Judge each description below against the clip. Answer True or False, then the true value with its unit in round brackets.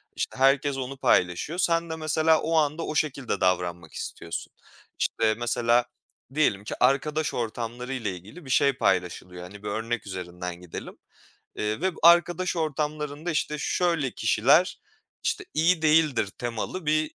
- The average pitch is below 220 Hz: True (135 Hz)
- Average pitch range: False (6.8 semitones)